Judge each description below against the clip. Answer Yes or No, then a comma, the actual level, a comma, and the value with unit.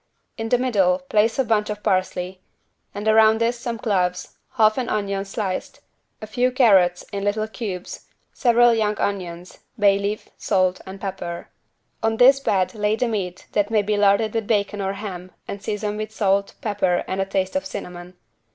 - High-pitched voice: Yes, high, 205 Hz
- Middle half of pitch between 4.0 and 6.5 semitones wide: No, average, 2.7 semitones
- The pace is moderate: Yes, average, 180 wpm